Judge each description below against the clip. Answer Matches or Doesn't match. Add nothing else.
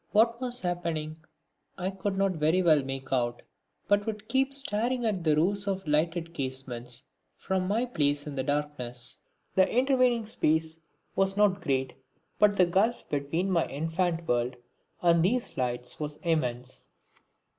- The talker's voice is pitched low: Doesn't match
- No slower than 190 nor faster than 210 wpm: Doesn't match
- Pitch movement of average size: Doesn't match